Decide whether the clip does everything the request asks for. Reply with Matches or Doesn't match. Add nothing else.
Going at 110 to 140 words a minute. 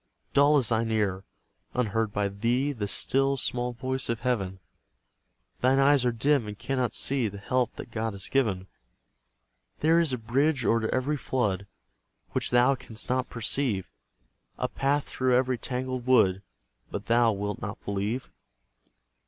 Doesn't match